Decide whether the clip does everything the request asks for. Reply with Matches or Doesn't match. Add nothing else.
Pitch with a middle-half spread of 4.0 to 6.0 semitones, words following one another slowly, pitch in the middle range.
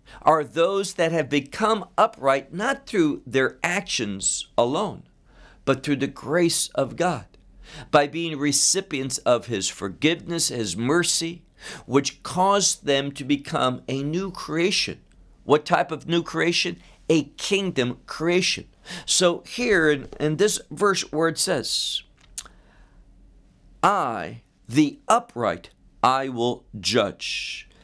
Matches